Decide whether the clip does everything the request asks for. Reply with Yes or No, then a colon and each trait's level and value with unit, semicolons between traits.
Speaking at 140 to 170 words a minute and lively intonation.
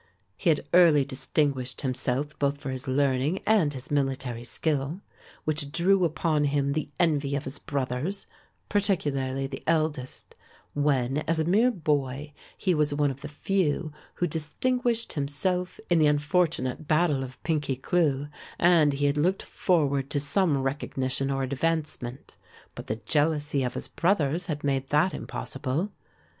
No: average, 150 wpm; average, 3.4 semitones